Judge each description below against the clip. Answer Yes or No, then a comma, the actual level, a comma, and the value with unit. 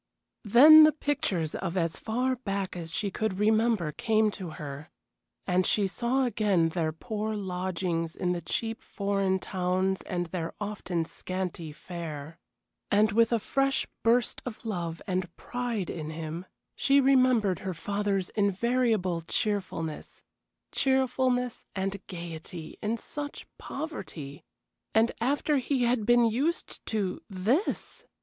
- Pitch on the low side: No, high, 200 Hz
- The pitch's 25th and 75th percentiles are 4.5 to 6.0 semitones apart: Yes, average, 5.1 semitones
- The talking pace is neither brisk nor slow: No, slow, 130 wpm